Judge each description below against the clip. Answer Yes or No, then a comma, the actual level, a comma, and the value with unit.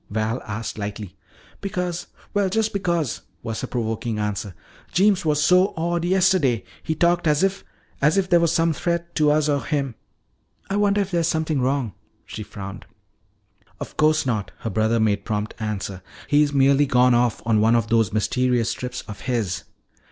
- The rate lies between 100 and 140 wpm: No, average, 175 wpm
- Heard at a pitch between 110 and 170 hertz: Yes, low, 135 Hz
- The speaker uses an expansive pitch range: Yes, wide, 7.6 semitones